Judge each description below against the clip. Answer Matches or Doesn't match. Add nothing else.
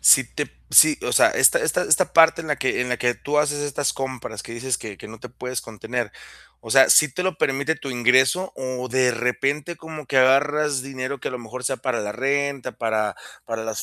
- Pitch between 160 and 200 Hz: Doesn't match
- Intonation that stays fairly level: Doesn't match